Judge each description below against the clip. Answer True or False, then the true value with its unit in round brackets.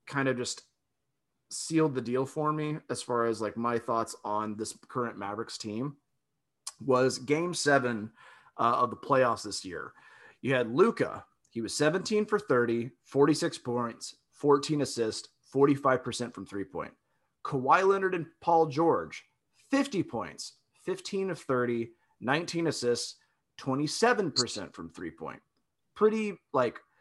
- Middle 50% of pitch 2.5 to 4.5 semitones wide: False (5.3 semitones)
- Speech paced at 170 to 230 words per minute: False (140 wpm)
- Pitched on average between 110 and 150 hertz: True (140 Hz)